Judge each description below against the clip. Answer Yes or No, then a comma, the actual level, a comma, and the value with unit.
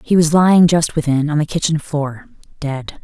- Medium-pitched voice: Yes, medium, 155 Hz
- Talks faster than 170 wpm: Yes, average, 200 wpm